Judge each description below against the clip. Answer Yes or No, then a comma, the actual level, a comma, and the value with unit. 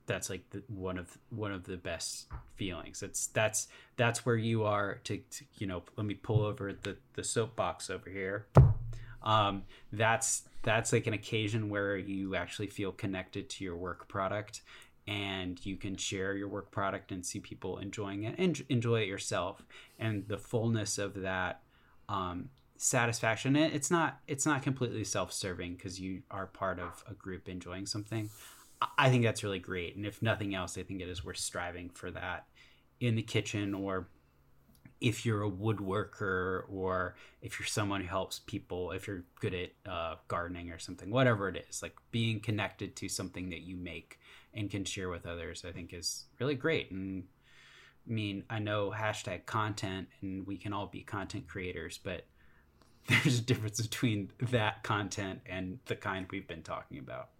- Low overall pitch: Yes, low, 100 Hz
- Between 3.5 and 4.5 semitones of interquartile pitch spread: No, average, 3.1 semitones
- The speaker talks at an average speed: Yes, average, 180 wpm